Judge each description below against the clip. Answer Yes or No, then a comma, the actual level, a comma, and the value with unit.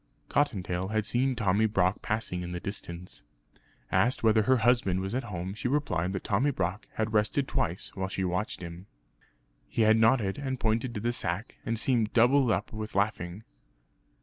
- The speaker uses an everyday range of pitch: Yes, average, 4.2 semitones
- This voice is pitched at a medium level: No, low, 110 Hz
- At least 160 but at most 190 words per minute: Yes, average, 175 wpm